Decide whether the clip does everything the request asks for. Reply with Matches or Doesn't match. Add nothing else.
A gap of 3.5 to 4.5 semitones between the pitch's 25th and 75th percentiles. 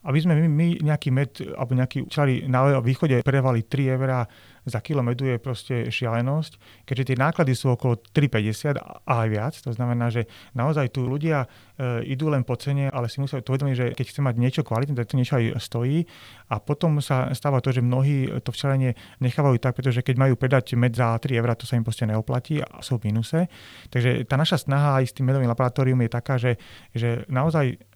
Doesn't match